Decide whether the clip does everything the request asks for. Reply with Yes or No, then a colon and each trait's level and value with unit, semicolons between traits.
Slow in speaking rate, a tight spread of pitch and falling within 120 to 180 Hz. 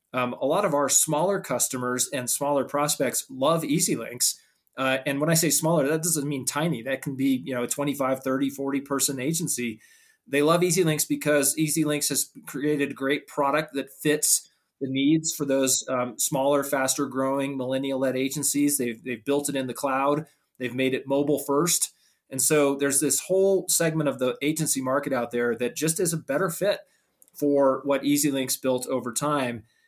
No: average, 190 wpm; narrow, 2.2 semitones; medium, 140 Hz